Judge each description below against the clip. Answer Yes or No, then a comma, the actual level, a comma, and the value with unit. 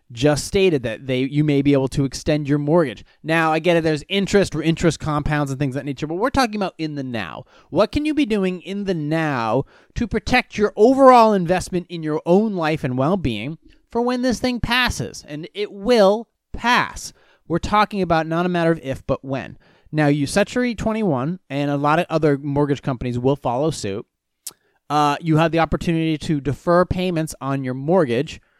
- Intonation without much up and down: No, average, 5.0 semitones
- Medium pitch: Yes, medium, 160 Hz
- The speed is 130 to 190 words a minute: No, average, 200 wpm